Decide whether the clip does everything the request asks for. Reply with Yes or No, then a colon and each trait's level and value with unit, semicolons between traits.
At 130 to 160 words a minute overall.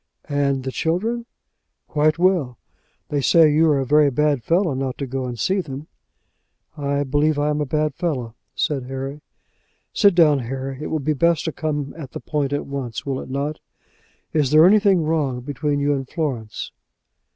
No: average, 185 wpm